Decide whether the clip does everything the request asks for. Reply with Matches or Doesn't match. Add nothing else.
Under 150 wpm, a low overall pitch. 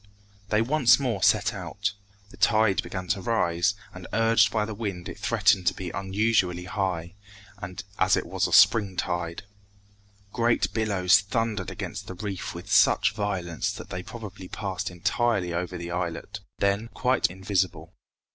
Doesn't match